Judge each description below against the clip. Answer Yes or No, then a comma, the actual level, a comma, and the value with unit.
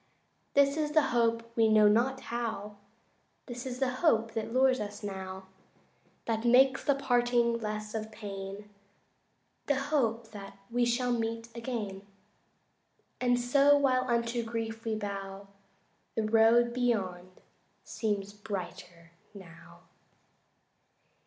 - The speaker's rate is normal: No, slow, 120 wpm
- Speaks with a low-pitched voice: No, high, 230 Hz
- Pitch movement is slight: No, average, 3.0 semitones